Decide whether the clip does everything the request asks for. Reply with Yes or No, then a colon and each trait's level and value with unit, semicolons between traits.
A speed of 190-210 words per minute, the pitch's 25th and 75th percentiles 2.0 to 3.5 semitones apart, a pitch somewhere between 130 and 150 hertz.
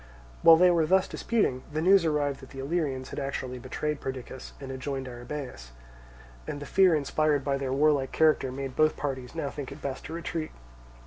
Yes: average, 195 wpm; average, 2.8 semitones; medium, 140 Hz